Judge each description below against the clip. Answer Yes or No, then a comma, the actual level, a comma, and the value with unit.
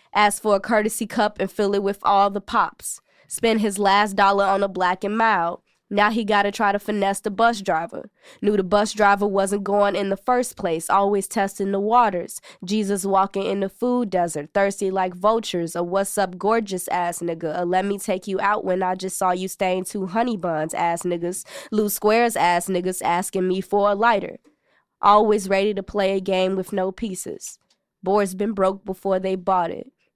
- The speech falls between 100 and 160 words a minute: No, average, 200 wpm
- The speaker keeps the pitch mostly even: Yes, narrow, 1.8 semitones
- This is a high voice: Yes, high, 200 Hz